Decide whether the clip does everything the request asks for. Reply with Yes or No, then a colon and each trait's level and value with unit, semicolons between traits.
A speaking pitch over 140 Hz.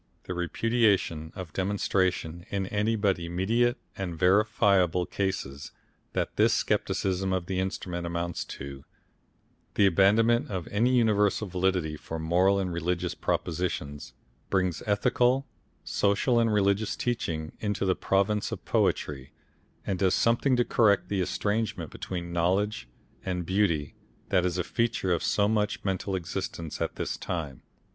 No: very low, 95 Hz